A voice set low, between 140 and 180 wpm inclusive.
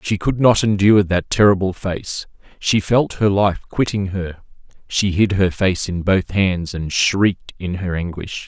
Yes: very low, 95 Hz; average, 175 wpm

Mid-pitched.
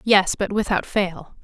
No: high, 195 Hz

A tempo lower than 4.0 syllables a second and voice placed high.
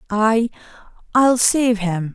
Yes: 3.1 syllables/s; high, 225 Hz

